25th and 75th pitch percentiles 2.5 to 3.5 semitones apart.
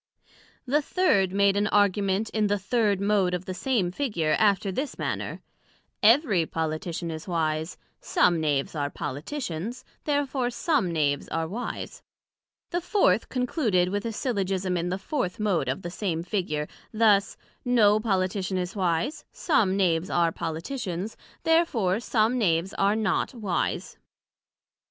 No: average, 4.7 semitones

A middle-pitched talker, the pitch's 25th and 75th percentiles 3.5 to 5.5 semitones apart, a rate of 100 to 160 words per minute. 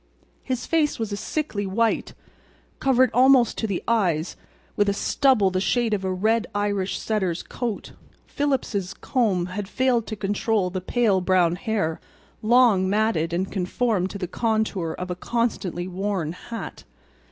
No: high, 205 Hz; average, 4.0 semitones; average, 150 wpm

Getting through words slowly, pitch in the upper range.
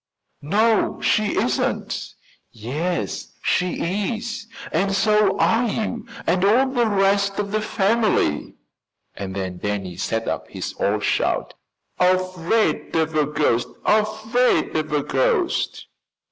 Yes: slow, 120 wpm; high, 195 Hz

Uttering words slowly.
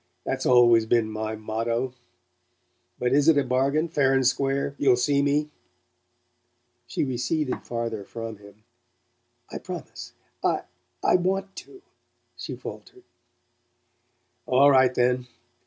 Yes: slow, 125 wpm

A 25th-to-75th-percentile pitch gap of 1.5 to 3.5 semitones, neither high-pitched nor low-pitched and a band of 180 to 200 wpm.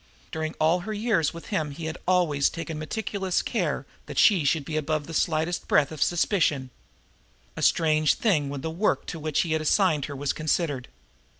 Yes: average, 2.7 semitones; medium, 160 Hz; average, 190 wpm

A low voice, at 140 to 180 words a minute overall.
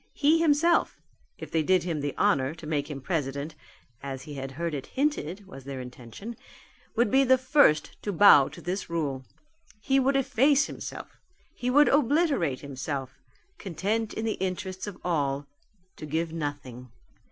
No: medium, 170 Hz; average, 165 wpm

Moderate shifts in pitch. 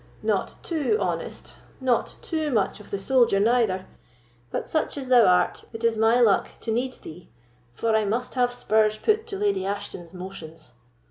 Yes: average, 4.5 semitones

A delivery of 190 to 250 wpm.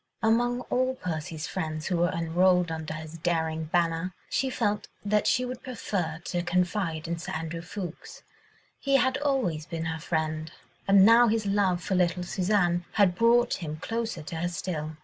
No: average, 170 wpm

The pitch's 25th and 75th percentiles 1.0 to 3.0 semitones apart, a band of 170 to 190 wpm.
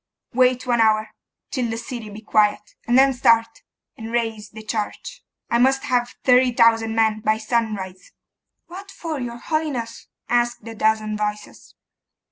No: narrow, 2.6 semitones; average, 150 wpm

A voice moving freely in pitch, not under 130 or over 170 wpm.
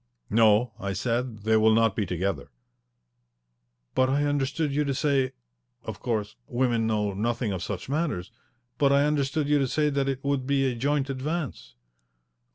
No: average, 4.4 semitones; average, 165 wpm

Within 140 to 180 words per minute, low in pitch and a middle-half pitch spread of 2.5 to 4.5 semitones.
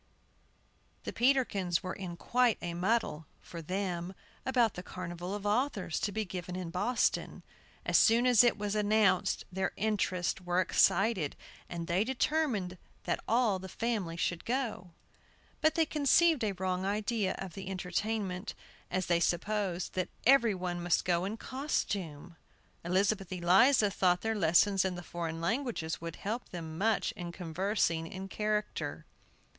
No: average, 150 wpm; high, 190 Hz; average, 3.9 semitones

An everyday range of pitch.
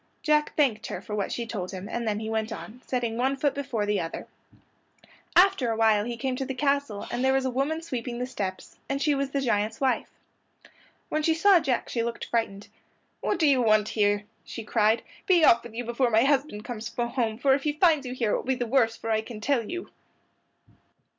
Yes: average, 3.9 semitones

